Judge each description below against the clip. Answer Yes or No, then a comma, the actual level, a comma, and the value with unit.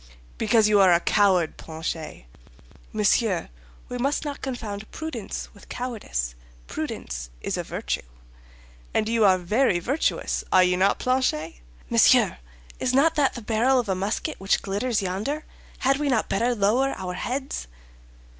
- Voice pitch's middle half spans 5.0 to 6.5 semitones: Yes, wide, 5.6 semitones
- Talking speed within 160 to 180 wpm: No, average, 150 wpm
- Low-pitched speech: No, high, 215 Hz